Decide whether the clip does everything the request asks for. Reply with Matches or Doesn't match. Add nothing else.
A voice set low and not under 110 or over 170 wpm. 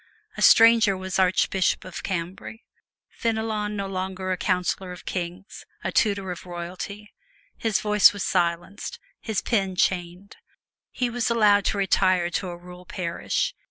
Doesn't match